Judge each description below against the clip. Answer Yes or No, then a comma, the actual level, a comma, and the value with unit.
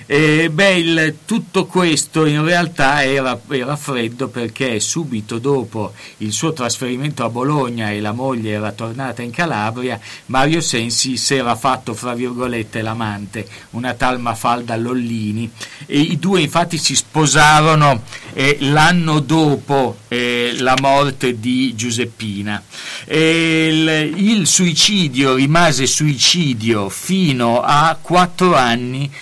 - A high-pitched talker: No, low, 130 Hz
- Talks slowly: No, average, 125 wpm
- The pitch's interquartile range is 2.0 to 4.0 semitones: No, average, 4.8 semitones